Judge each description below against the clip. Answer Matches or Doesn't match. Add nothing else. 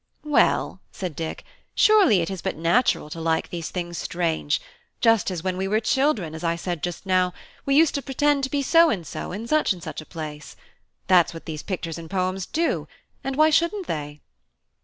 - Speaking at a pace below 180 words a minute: Doesn't match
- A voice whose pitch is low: Doesn't match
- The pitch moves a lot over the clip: Matches